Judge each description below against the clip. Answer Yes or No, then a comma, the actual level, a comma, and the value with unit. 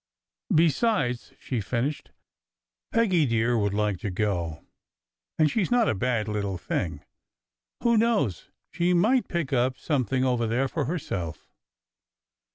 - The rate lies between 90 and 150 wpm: Yes, average, 140 wpm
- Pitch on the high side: No, low, 125 Hz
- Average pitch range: No, wide, 8.3 semitones